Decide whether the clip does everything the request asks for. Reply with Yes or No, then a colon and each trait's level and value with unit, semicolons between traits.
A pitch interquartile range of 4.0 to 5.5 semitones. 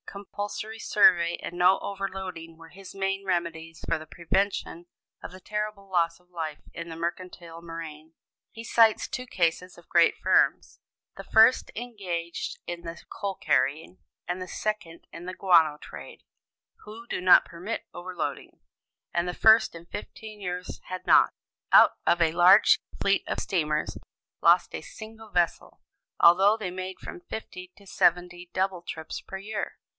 No: average, 2.8 semitones